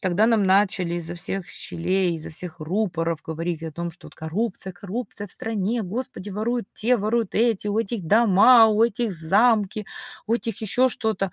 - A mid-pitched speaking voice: No, high, 200 Hz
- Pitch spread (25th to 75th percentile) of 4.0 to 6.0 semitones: Yes, average, 4.3 semitones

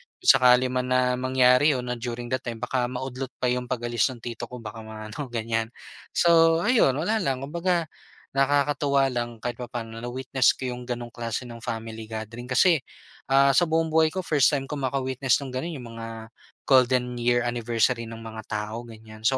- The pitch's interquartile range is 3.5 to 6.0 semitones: No, average, 2.7 semitones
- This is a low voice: Yes, low, 125 Hz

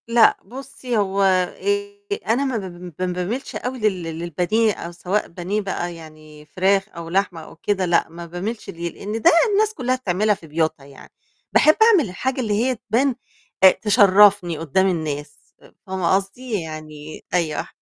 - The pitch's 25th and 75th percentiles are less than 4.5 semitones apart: No, average, 4.9 semitones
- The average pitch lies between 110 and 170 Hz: No, high, 190 Hz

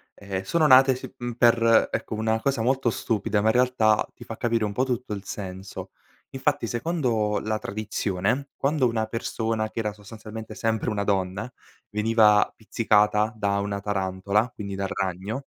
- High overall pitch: No, low, 110 Hz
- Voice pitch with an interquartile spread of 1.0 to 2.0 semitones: No, narrow, 2.6 semitones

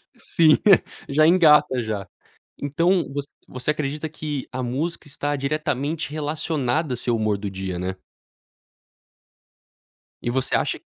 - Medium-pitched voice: Yes, medium, 145 Hz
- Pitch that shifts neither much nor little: Yes, average, 4.0 semitones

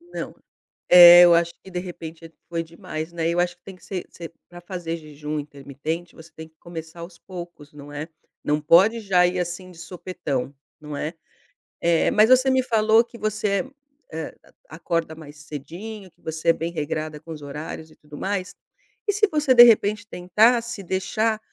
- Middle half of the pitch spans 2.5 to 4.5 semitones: Yes, average, 3.9 semitones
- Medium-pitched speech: Yes, medium, 170 Hz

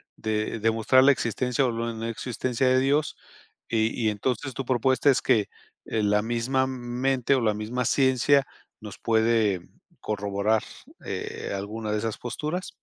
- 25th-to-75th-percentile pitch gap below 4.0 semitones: Yes, average, 3.1 semitones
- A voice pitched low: Yes, low, 115 Hz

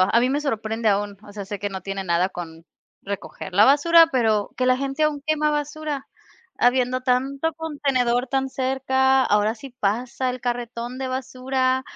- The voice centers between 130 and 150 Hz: No, very high, 255 Hz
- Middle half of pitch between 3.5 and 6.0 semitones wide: Yes, average, 4.0 semitones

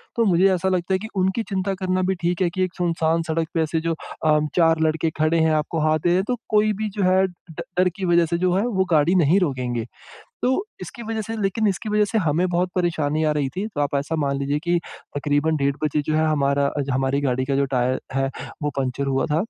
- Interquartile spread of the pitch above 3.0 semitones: Yes, average, 4.4 semitones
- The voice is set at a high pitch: No, medium, 165 Hz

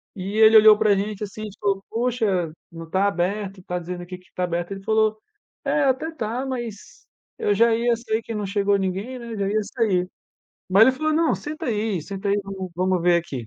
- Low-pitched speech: No, high, 205 Hz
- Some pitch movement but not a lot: Yes, average, 3.3 semitones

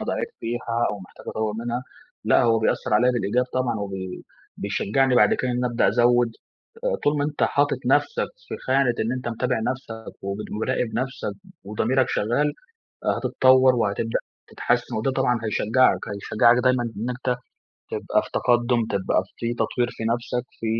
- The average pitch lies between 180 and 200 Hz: No, low, 120 Hz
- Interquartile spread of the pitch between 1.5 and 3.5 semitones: Yes, narrow, 2.4 semitones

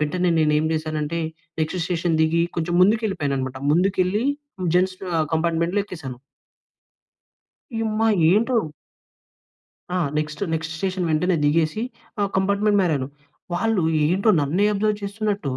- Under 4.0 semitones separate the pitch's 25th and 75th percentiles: No, average, 4.3 semitones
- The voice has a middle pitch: Yes, medium, 175 Hz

